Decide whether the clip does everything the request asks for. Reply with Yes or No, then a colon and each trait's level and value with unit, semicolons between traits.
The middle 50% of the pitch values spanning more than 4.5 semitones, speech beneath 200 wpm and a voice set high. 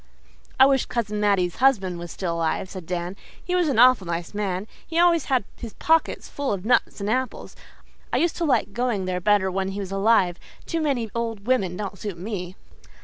No: wide, 5.5 semitones; fast, 205 wpm; high, 205 Hz